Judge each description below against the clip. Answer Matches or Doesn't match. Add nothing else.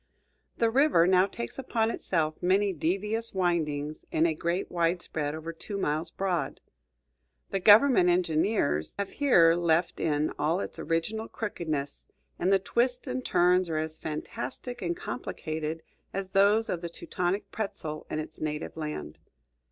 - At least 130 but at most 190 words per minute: Matches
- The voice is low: Doesn't match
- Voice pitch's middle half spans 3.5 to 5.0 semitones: Matches